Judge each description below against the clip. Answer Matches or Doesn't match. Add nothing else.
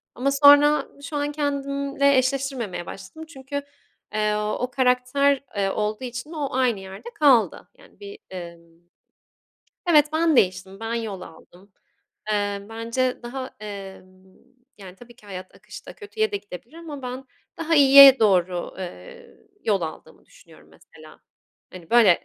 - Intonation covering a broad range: Matches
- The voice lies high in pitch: Matches